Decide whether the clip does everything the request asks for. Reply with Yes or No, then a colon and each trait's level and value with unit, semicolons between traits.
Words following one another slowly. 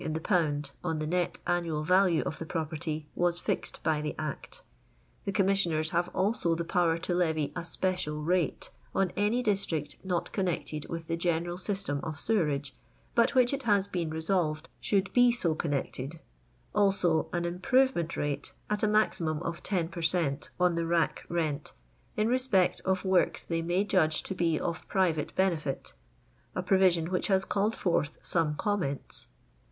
No: average, 170 wpm